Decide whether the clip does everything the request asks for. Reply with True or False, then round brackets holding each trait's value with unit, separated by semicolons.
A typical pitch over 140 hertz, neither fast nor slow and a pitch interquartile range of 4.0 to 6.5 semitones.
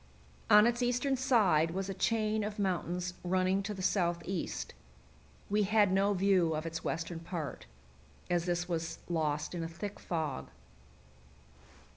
False (185 Hz; 145 wpm; 3.5 semitones)